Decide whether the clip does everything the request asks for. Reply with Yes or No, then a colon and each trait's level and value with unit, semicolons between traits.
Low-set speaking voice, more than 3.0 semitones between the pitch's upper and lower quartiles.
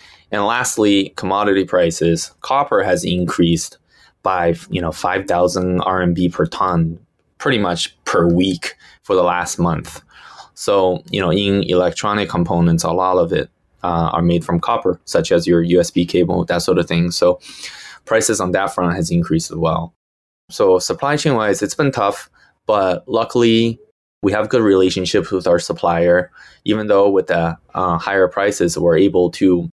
No: very low, 90 Hz; average, 2.7 semitones